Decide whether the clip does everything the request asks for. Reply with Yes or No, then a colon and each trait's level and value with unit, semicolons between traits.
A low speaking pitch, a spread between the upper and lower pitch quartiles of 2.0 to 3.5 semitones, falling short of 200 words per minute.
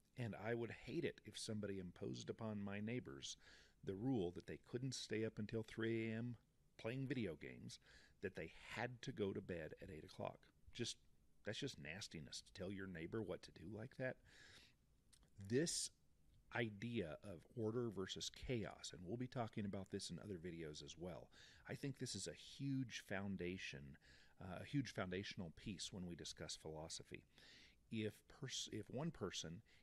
No: low, 105 Hz; average, 4.2 semitones; average, 170 wpm